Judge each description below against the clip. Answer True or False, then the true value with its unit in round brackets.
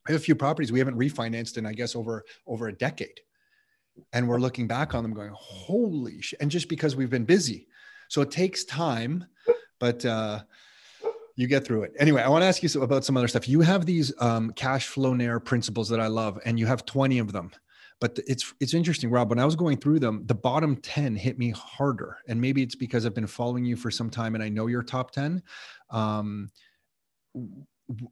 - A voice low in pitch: True (130 Hz)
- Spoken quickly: True (220 wpm)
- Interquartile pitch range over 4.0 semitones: True (4.6 semitones)